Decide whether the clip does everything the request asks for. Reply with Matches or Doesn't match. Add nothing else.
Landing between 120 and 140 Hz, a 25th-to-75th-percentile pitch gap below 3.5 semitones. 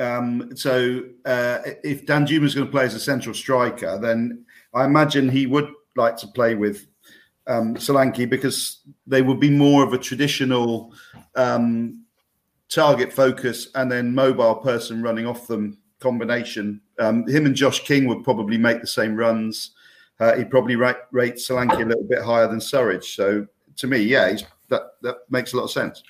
Matches